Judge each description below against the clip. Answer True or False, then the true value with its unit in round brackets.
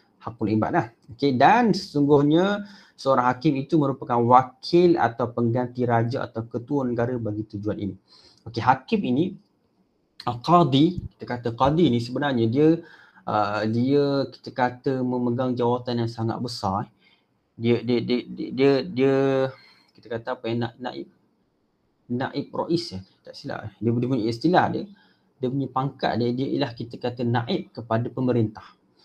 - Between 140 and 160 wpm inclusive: True (150 wpm)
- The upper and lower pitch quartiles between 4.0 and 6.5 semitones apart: False (2.8 semitones)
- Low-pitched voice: True (125 Hz)